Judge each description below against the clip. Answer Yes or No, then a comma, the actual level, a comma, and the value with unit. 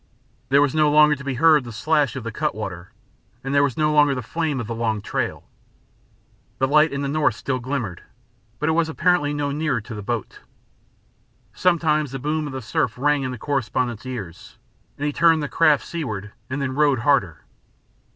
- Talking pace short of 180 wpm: No, average, 200 wpm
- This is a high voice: No, medium, 140 Hz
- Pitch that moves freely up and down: No, average, 4.1 semitones